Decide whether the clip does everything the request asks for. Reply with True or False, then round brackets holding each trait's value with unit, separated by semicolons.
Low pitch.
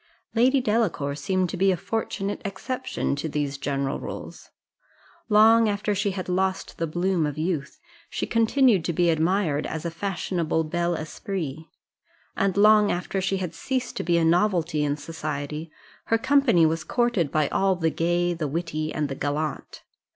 False (175 Hz)